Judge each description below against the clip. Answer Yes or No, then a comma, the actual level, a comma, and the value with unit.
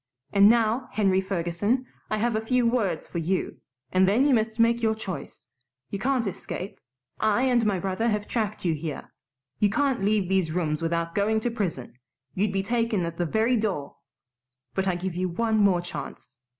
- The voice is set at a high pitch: Yes, high, 205 Hz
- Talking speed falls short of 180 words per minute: No, average, 185 wpm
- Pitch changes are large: No, average, 4.2 semitones